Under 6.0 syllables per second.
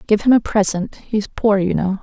Yes: 4.8 syllables/s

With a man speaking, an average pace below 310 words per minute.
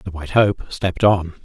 Yes: male; fast, 210 wpm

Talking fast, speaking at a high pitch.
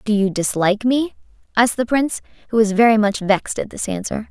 Yes: fast, 210 wpm; high, 220 Hz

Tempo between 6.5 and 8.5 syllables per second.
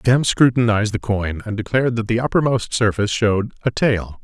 No: 5.8 syllables/s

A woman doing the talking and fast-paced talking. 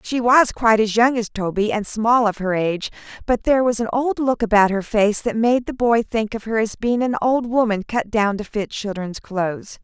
Yes: female; fast, 240 wpm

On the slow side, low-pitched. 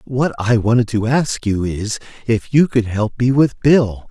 No: fast, 205 wpm; low, 115 Hz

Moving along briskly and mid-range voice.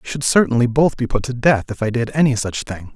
No: fast, 285 wpm; low, 125 Hz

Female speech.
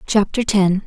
Yes: female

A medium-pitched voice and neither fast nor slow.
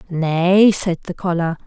Yes: medium, 175 Hz; average, 145 wpm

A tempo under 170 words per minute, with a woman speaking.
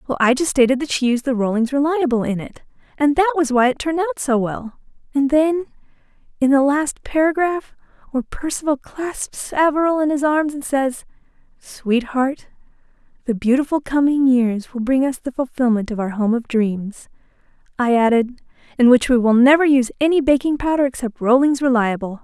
No: average, 175 wpm; female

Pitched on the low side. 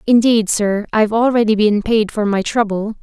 No: high, 215 Hz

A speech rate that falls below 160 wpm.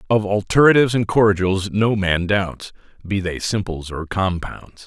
Yes: average, 150 wpm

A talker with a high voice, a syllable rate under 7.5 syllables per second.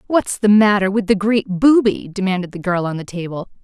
Yes: high, 200 Hz; 5.4 syllables/s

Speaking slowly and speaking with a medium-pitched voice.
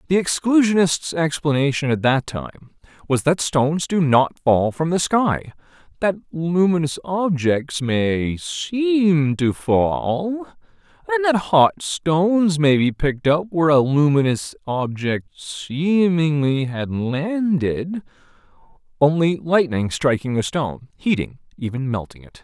Yes: slow, 120 wpm; medium, 155 Hz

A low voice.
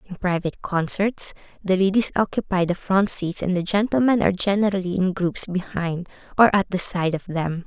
No: high, 190 Hz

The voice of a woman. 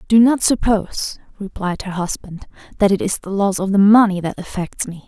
Yes: female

